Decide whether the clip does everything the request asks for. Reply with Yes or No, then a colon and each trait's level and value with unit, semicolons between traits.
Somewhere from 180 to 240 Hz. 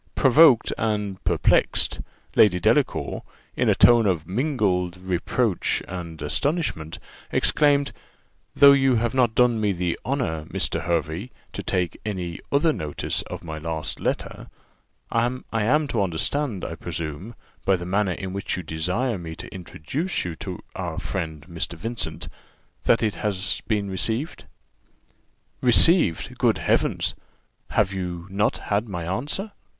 No: low, 100 Hz